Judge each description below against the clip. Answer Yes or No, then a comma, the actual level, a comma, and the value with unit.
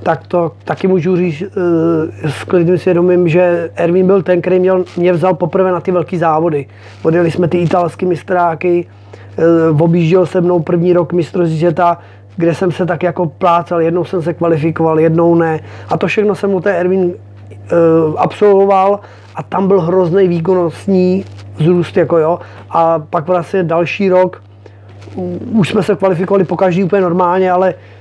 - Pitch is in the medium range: Yes, medium, 175 Hz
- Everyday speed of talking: Yes, average, 155 wpm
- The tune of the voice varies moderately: No, narrow, 2.1 semitones